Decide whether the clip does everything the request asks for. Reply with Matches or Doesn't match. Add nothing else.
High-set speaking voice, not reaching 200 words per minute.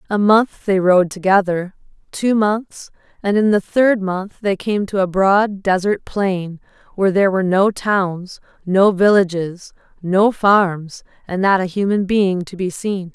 Matches